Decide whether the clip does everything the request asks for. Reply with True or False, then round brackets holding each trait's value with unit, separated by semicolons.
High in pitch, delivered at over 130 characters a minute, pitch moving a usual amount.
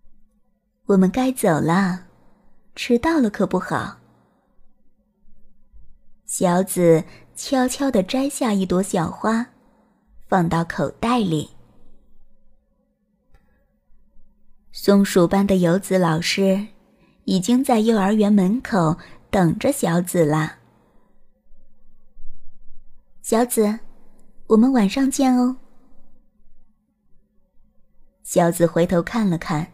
False (205 Hz; 125 characters per minute; 4.7 semitones)